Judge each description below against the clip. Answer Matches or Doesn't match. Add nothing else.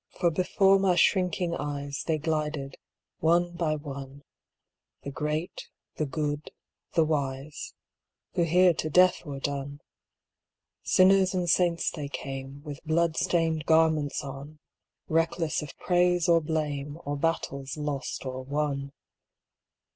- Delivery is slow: Matches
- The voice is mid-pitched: Matches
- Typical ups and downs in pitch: Matches